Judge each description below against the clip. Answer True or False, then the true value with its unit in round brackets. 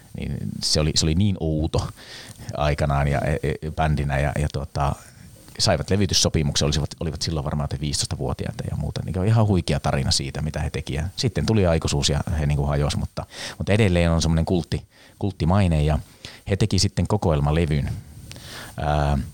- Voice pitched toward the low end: True (80 Hz)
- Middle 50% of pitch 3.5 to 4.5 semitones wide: True (4.0 semitones)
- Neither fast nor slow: False (160 wpm)